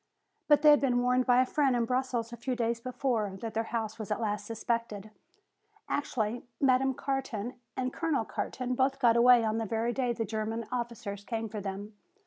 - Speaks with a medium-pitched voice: No, high, 235 Hz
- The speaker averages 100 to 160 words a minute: No, average, 195 wpm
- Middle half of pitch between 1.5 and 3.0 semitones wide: Yes, narrow, 2.4 semitones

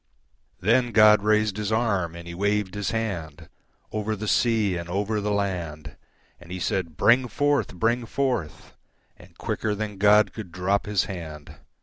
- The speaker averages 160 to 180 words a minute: No, average, 145 wpm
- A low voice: Yes, low, 105 Hz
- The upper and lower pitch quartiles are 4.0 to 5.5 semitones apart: No, average, 3.5 semitones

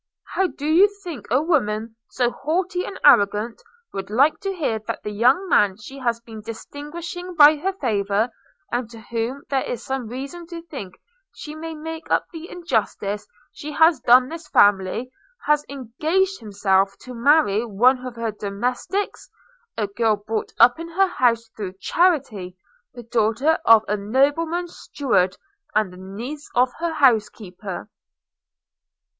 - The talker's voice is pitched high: Yes, very high, 250 Hz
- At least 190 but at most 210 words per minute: No, average, 155 wpm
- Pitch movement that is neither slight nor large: No, wide, 6.7 semitones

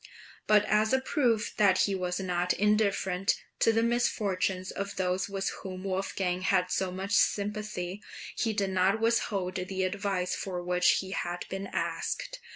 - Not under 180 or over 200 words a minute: No, average, 160 wpm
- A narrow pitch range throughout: Yes, narrow, 2.3 semitones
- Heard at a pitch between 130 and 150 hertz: No, high, 195 Hz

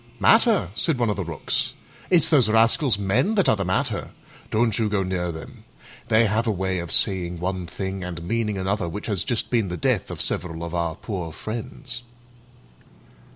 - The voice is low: Yes, low, 100 Hz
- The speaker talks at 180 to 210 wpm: Yes, average, 190 wpm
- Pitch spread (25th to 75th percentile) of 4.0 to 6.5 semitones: Yes, average, 4.5 semitones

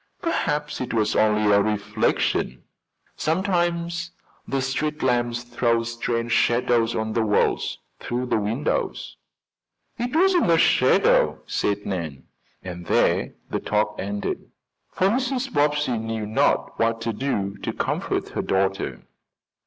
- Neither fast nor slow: No, slow, 130 wpm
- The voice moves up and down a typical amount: No, wide, 6.0 semitones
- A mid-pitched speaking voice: No, low, 115 Hz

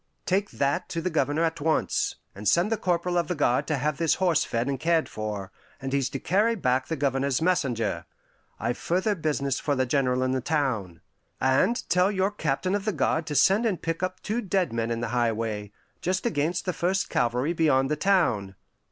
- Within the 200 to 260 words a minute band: Yes, fast, 205 wpm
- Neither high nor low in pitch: Yes, medium, 150 Hz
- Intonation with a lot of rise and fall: Yes, wide, 5.9 semitones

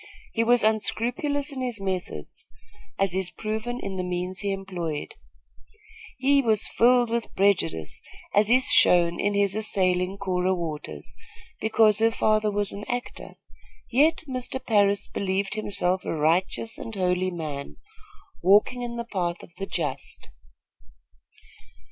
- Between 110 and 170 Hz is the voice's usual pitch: No, high, 200 Hz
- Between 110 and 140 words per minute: Yes, slow, 135 wpm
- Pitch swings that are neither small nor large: Yes, average, 3.9 semitones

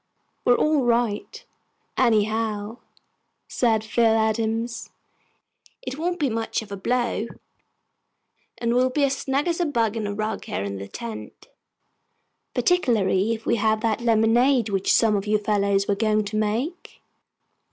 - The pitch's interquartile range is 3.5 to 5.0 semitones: No, narrow, 2.4 semitones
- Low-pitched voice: No, high, 225 Hz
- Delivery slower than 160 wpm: Yes, average, 150 wpm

